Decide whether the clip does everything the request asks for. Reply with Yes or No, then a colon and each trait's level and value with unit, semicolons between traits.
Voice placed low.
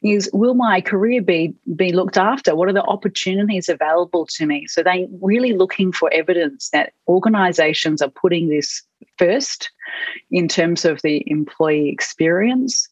No: medium, 180 Hz